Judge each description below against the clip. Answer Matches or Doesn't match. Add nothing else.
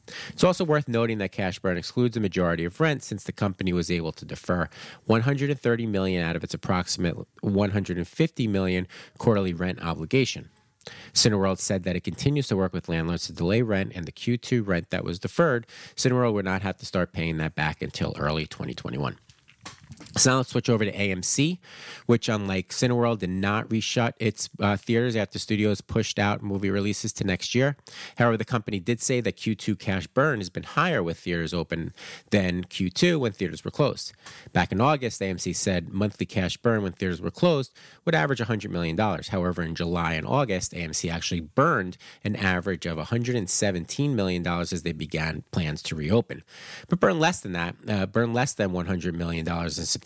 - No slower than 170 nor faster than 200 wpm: Matches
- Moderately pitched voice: Doesn't match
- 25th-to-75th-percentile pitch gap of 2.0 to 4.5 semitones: Doesn't match